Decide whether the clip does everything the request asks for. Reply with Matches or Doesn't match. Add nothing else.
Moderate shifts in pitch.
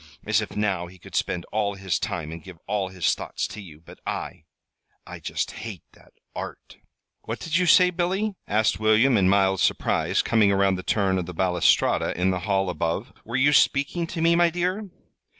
Doesn't match